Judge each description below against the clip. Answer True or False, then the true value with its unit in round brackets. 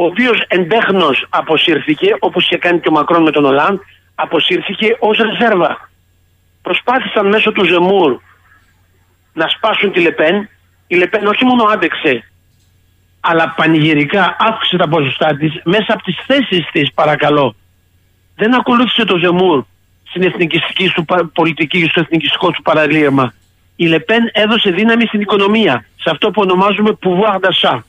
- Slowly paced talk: False (140 wpm)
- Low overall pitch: False (175 Hz)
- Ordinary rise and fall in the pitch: False (6.4 semitones)